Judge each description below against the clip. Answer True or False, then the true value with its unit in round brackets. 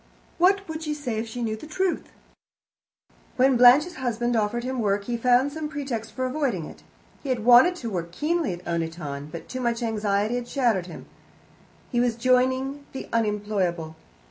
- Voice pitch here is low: False (240 Hz)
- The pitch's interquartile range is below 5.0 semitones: True (4.3 semitones)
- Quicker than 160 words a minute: True (170 wpm)